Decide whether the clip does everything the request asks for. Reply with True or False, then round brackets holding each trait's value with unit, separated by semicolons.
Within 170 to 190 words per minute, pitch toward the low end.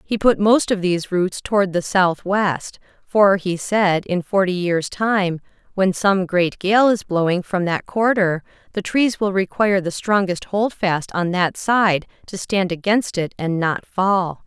False (175 wpm; 190 Hz)